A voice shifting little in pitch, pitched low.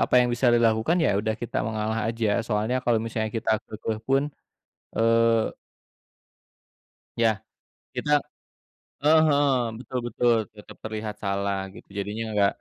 Yes: narrow, 2.0 semitones; low, 115 Hz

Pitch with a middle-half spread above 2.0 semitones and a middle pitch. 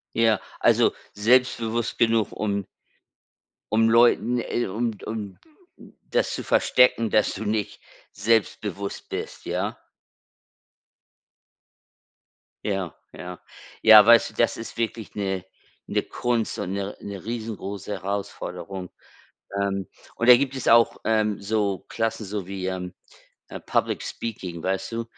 No: average, 2.8 semitones; low, 110 Hz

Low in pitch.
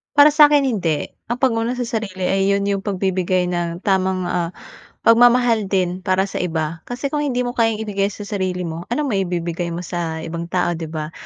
No: high, 190 Hz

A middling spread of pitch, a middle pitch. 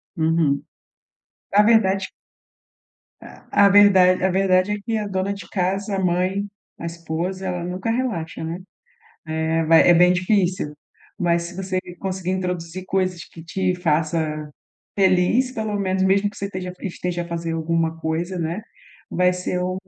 No: narrow, 2.3 semitones; medium, 180 Hz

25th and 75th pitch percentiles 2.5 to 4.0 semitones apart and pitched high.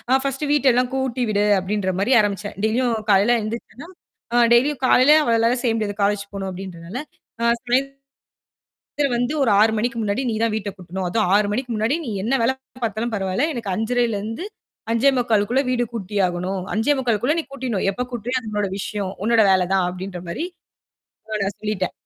Yes: average, 3.7 semitones; high, 225 Hz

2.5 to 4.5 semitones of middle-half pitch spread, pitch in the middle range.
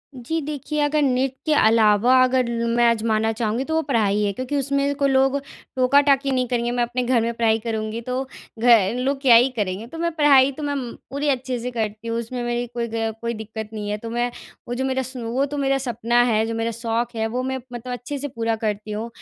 No: average, 2.8 semitones; high, 240 Hz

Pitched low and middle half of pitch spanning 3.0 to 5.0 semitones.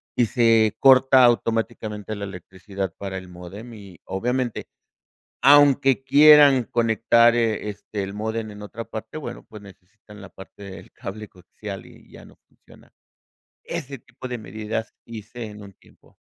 Yes: low, 110 Hz; average, 3.3 semitones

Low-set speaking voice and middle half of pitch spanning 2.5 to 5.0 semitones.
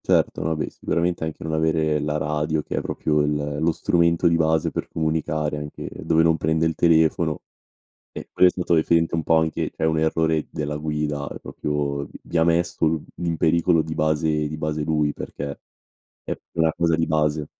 No: very low, 80 Hz; narrow, 1.3 semitones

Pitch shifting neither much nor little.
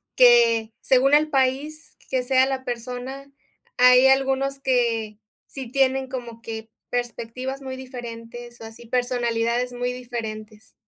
No: narrow, 2.2 semitones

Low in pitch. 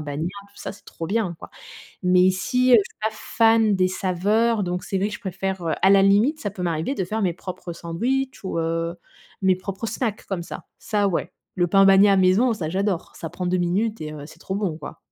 No: high, 190 Hz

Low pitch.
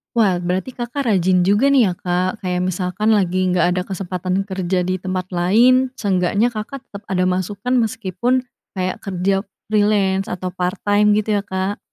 No: high, 190 Hz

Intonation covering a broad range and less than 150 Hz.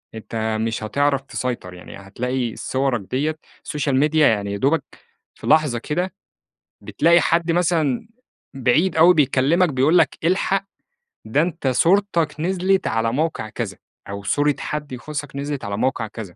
Yes: wide, 5.8 semitones; medium, 140 Hz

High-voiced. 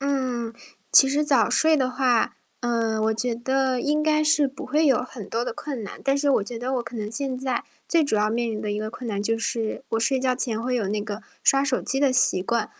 Yes: very high, 250 Hz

